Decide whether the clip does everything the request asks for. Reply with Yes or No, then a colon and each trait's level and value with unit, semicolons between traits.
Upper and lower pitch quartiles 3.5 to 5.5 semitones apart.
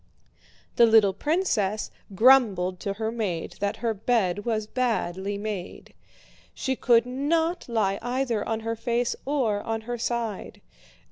No: average, 3.1 semitones